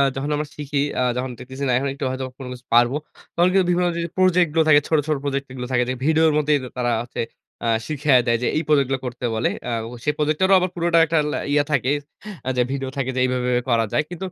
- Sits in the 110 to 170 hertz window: Yes, medium, 140 Hz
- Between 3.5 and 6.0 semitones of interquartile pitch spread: Yes, average, 3.8 semitones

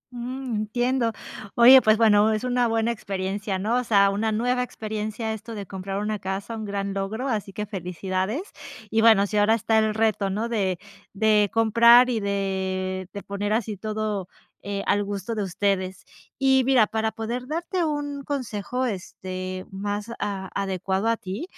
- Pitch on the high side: Yes, high, 215 Hz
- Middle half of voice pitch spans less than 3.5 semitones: Yes, average, 2.8 semitones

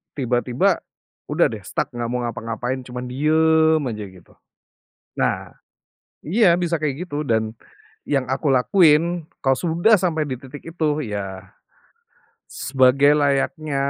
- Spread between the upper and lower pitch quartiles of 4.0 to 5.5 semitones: Yes, average, 4.3 semitones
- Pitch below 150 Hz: Yes, medium, 140 Hz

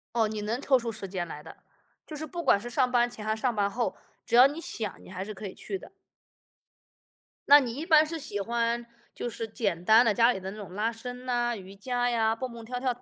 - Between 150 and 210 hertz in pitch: No, high, 235 Hz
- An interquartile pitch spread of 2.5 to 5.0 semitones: Yes, average, 3.1 semitones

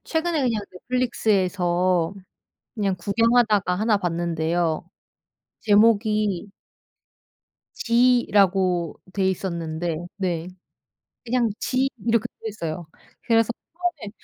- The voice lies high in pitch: Yes, high, 200 Hz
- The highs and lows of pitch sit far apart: No, average, 4.8 semitones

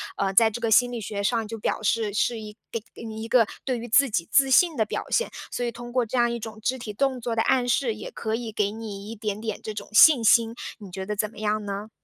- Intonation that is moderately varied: No, narrow, 2.3 semitones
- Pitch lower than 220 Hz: No, high, 225 Hz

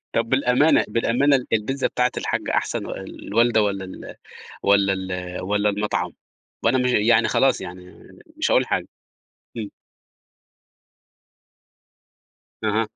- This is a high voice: No, low, 110 Hz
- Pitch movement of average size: Yes, average, 4.2 semitones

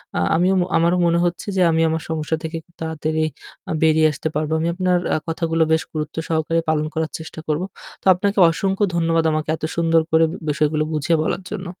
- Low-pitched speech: No, medium, 160 Hz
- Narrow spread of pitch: Yes, narrow, 1.3 semitones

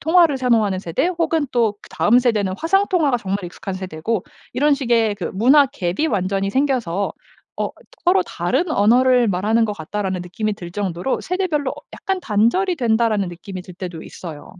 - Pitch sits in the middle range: No, high, 225 Hz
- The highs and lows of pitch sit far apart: Yes, wide, 7.0 semitones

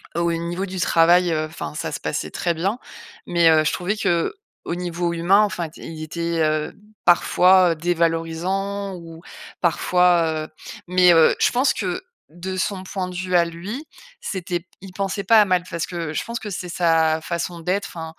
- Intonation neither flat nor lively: No, narrow, 2.1 semitones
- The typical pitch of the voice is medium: Yes, medium, 175 Hz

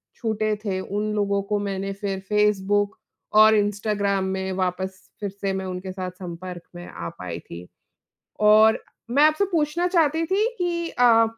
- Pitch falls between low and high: No, high, 205 Hz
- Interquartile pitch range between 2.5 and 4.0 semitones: Yes, average, 2.8 semitones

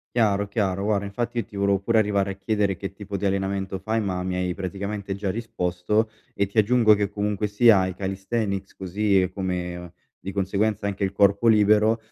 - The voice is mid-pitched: No, low, 100 Hz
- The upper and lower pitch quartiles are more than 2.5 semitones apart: No, narrow, 1.7 semitones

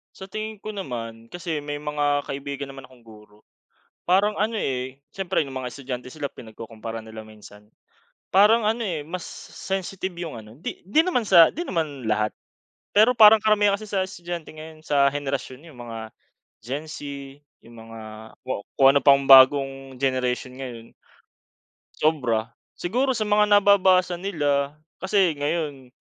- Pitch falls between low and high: Yes, medium, 145 Hz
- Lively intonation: Yes, wide, 7.1 semitones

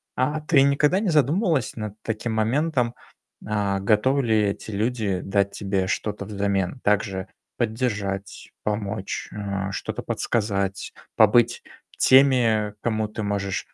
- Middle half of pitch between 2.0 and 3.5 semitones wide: No, average, 3.9 semitones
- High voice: No, low, 110 Hz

